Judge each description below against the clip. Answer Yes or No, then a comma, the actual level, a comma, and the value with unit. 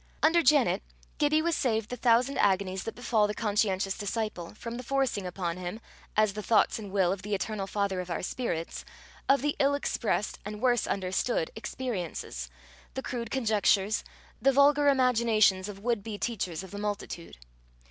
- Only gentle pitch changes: No, average, 4.4 semitones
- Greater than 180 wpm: No, average, 170 wpm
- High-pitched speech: Yes, high, 215 Hz